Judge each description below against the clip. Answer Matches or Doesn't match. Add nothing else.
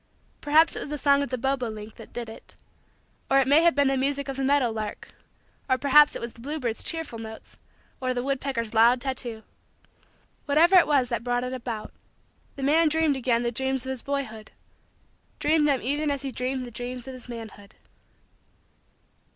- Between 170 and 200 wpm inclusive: Matches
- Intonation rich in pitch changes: Doesn't match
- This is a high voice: Matches